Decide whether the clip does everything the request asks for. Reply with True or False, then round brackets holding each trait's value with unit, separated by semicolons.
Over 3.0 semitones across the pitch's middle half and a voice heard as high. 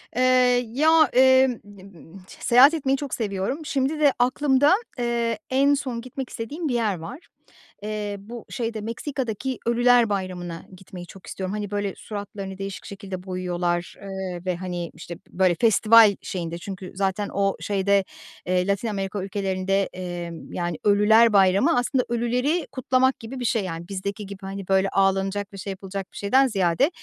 True (4.4 semitones; 205 Hz)